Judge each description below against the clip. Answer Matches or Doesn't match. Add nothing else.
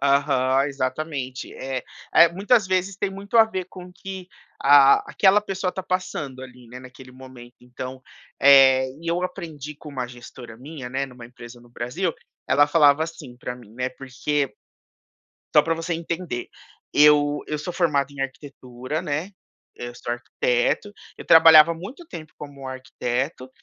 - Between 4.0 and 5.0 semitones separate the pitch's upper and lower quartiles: Matches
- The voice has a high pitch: Doesn't match